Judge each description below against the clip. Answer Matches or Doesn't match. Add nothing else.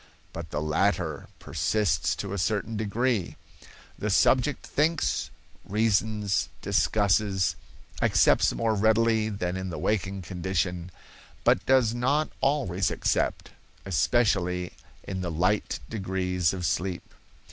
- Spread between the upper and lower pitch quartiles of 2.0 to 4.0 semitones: Matches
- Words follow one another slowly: Matches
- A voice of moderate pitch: Doesn't match